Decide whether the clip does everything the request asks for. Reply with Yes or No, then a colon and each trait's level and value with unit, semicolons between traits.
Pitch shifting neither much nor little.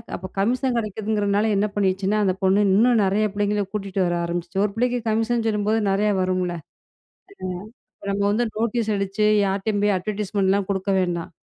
No: narrow, 2.0 semitones